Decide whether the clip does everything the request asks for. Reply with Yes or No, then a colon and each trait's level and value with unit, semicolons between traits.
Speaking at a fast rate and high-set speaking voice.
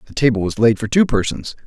No: fast, 250 wpm; low, 115 Hz